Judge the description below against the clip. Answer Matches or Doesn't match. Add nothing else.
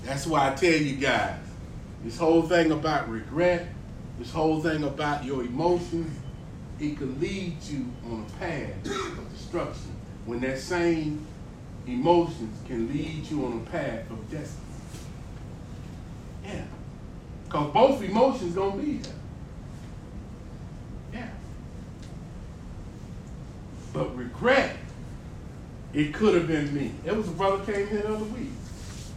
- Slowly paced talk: Matches